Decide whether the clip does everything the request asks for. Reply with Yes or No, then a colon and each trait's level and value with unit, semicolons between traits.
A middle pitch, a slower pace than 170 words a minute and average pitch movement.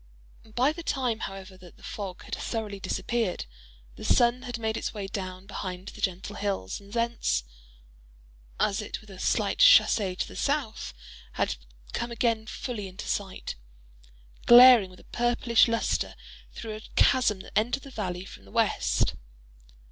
No: high, 215 Hz; average, 160 wpm; average, 3.9 semitones